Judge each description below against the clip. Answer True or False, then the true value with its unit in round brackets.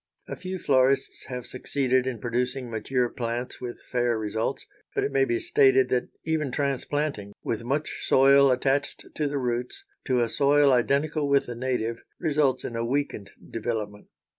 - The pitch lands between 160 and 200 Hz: False (130 Hz)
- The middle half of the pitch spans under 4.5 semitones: True (2.7 semitones)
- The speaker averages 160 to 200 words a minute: True (165 wpm)